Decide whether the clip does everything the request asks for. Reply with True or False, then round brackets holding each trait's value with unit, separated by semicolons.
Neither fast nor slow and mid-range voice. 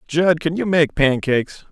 True (175 wpm; 150 Hz)